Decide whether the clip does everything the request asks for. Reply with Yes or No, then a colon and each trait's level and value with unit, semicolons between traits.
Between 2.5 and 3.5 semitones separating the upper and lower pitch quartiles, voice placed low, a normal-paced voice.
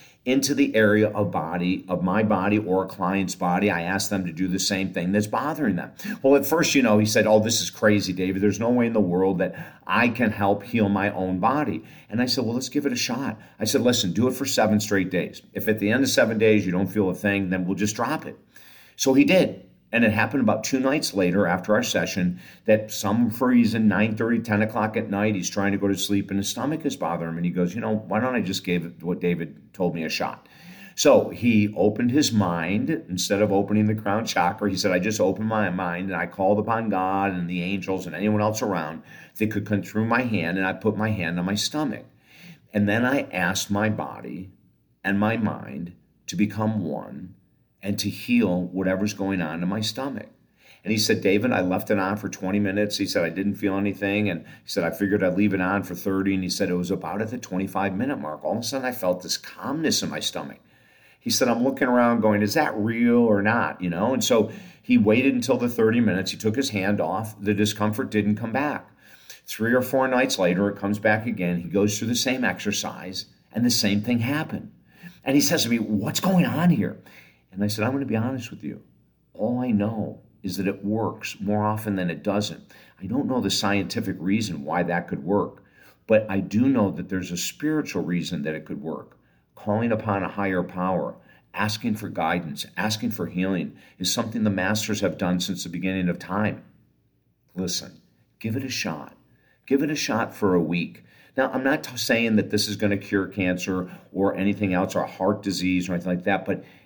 No: average, 2.8 semitones; low, 105 Hz; fast, 230 wpm